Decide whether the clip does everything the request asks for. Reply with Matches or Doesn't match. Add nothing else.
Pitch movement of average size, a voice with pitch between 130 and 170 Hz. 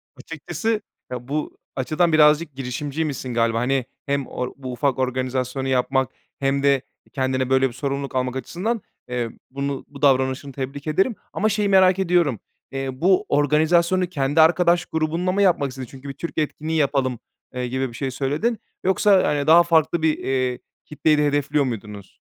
Matches